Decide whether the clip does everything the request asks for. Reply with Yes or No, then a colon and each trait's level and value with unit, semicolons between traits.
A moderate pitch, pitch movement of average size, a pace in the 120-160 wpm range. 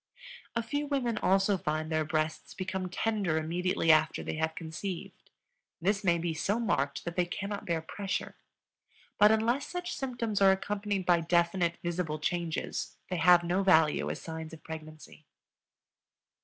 Yes: medium, 175 Hz; average, 4.1 semitones; average, 155 wpm